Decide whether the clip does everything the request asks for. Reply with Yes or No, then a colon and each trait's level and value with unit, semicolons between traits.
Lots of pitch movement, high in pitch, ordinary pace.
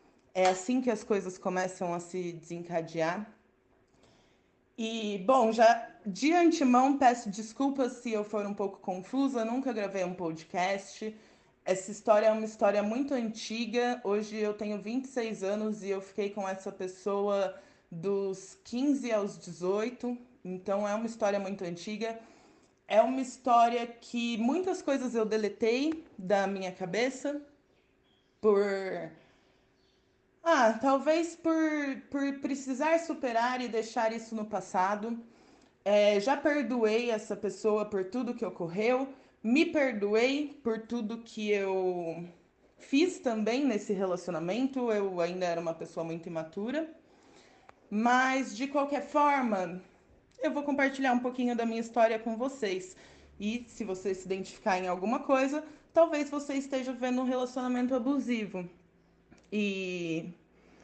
No: average, 4.8 semitones; high, 225 Hz; average, 130 wpm